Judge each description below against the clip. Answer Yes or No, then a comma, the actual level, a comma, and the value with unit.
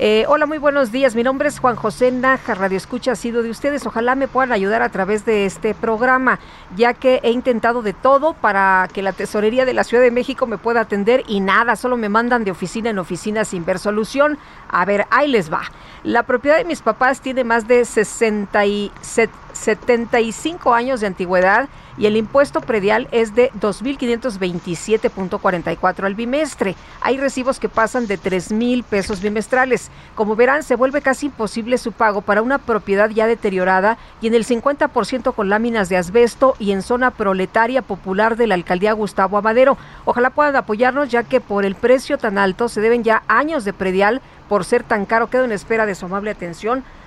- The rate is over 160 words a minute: Yes, fast, 190 wpm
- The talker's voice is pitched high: Yes, high, 230 Hz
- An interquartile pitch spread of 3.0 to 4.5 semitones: Yes, average, 3.5 semitones